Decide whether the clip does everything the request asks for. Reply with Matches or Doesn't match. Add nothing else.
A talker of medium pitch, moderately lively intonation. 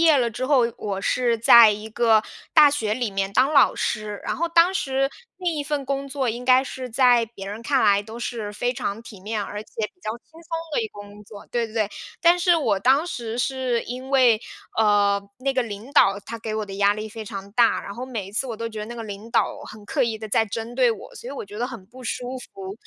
Doesn't match